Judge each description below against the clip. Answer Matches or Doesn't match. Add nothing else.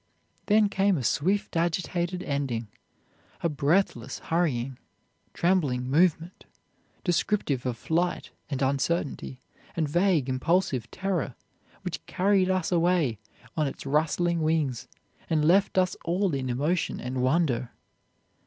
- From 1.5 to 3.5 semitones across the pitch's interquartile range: Doesn't match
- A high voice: Doesn't match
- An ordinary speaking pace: Doesn't match